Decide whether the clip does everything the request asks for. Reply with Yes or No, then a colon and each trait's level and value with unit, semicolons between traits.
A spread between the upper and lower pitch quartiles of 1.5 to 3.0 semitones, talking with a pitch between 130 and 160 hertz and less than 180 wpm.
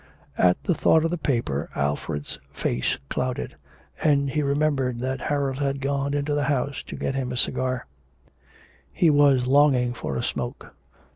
Yes: narrow, 2.5 semitones; low, 135 Hz; average, 160 wpm